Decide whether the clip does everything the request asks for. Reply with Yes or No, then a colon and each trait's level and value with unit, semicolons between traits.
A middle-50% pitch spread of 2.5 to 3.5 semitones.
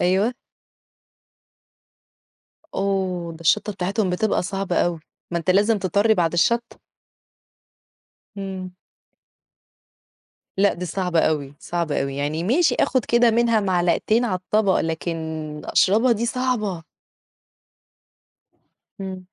No: average, 3.9 semitones